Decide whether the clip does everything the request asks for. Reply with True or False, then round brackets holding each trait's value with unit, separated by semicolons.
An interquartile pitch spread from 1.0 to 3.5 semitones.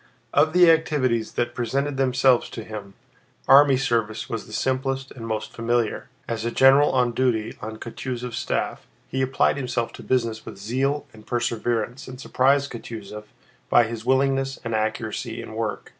True (3.0 semitones)